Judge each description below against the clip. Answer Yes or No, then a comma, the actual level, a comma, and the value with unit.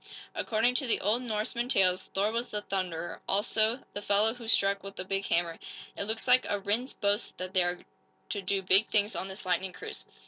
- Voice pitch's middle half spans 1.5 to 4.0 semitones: Yes, average, 2.8 semitones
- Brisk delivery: Yes, fast, 210 wpm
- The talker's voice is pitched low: No, high, 205 Hz